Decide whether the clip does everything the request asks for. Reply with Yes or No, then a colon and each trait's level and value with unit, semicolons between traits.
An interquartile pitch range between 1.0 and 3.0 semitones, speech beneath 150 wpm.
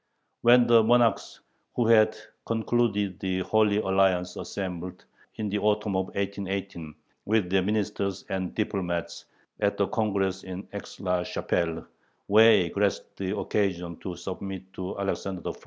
Yes: narrow, 2.4 semitones; average, 140 wpm